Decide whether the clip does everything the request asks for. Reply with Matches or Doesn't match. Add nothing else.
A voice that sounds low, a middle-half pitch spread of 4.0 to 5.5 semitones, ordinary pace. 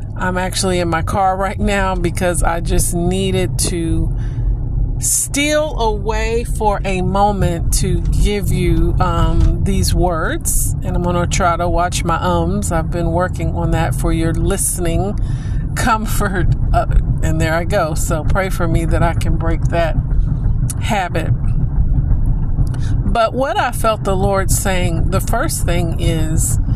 Matches